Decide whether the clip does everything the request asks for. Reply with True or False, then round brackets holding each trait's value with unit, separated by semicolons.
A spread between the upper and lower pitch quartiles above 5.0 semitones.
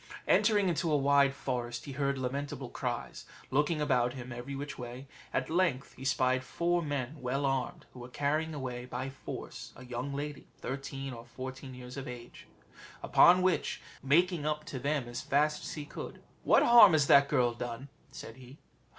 False (2.9 semitones)